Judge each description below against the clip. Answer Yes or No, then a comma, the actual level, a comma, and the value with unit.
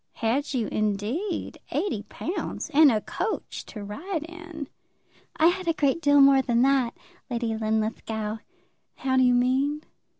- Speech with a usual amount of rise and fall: No, wide, 5.8 semitones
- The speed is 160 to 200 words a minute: No, average, 145 wpm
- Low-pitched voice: No, very high, 265 Hz